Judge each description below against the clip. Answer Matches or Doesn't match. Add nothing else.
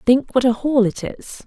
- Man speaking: Doesn't match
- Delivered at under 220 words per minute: Doesn't match